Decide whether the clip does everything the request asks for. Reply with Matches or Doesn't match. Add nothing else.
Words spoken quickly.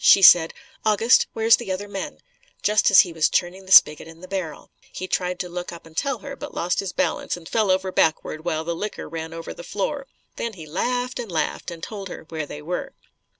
Matches